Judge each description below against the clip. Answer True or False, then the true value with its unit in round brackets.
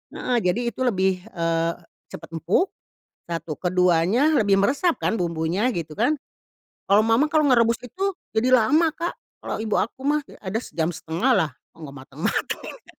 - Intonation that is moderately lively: False (7.2 semitones)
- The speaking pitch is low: False (205 Hz)